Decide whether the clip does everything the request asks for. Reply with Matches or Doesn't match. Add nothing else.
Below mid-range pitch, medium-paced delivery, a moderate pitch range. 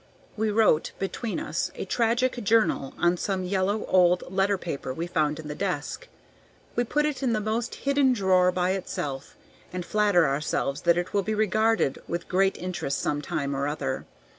Doesn't match